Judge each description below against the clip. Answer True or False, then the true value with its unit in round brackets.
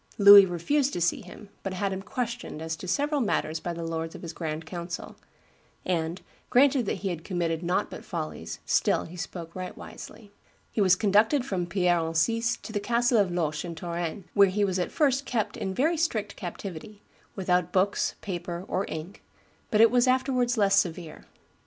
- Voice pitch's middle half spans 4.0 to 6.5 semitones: True (4.4 semitones)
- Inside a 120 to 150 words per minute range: False (190 wpm)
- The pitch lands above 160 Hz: True (190 Hz)